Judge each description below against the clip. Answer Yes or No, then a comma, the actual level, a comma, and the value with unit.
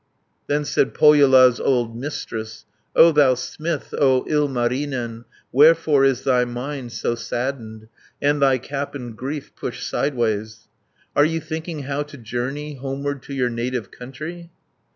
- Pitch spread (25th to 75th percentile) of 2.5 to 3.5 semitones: Yes, average, 3.2 semitones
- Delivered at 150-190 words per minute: No, slow, 135 wpm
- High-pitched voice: No, low, 135 Hz